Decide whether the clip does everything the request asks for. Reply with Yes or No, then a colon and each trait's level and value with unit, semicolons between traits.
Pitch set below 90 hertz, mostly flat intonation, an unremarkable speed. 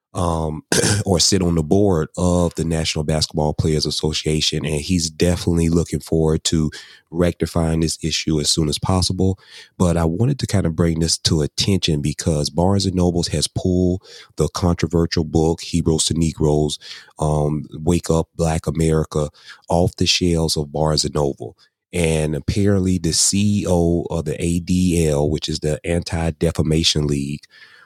Yes: very low, 80 Hz; narrow, 2.3 semitones; average, 155 wpm